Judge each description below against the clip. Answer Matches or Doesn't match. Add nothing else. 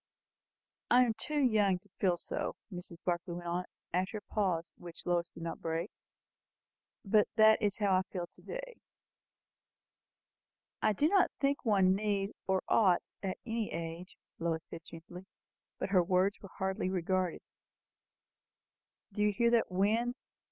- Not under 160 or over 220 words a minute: Doesn't match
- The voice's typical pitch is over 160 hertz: Matches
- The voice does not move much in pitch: Doesn't match